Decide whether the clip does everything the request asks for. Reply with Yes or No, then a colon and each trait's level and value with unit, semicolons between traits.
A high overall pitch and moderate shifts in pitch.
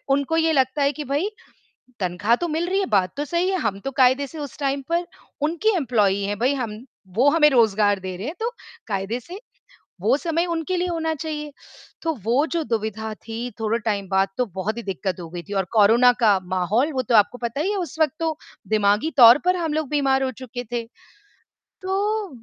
No: very high, 255 Hz; wide, 6.7 semitones